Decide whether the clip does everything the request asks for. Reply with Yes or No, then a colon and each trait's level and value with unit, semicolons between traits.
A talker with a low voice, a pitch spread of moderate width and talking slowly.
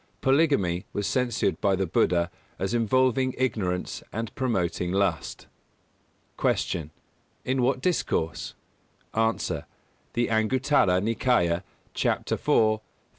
No: low, 110 Hz; wide, 6.0 semitones; slow, 110 wpm